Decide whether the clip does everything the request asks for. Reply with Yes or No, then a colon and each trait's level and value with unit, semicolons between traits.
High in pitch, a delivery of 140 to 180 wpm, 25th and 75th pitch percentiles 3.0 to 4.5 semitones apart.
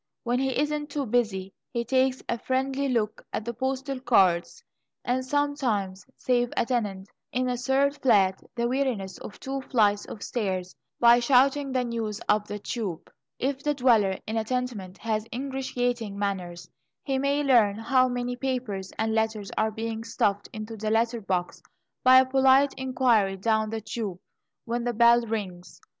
Yes: high, 235 Hz; average, 165 wpm; average, 3.7 semitones